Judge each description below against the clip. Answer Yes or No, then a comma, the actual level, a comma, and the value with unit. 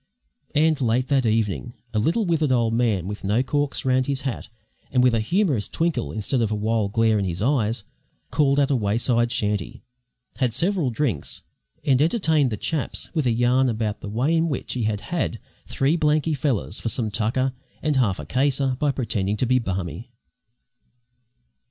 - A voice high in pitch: No, low, 125 Hz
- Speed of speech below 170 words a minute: No, average, 180 wpm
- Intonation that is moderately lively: Yes, average, 4.6 semitones